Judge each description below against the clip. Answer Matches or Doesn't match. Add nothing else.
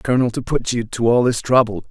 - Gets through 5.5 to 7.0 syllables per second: Matches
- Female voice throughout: Doesn't match